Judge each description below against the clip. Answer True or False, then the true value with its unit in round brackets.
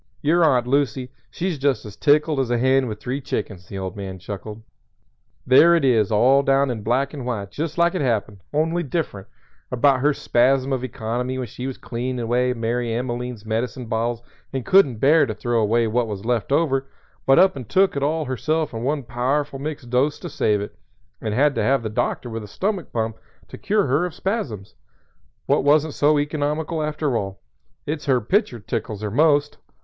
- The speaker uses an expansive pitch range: False (4.3 semitones)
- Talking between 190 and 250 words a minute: True (195 wpm)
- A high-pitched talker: False (130 Hz)